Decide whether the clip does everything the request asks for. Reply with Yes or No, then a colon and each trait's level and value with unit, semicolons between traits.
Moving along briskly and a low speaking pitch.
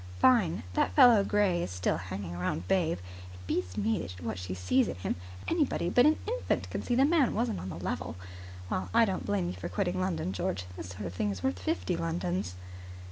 Yes: fast, 210 wpm; very low, 95 Hz